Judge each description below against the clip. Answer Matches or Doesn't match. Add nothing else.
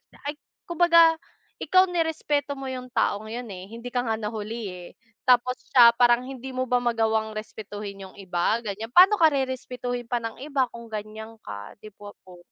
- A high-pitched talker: Matches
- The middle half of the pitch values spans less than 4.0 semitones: Matches